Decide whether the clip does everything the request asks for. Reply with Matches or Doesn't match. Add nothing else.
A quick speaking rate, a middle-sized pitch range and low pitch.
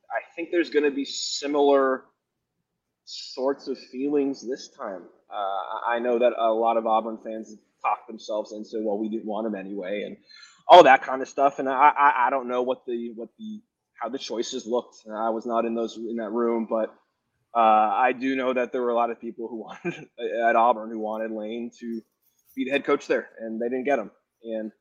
Matches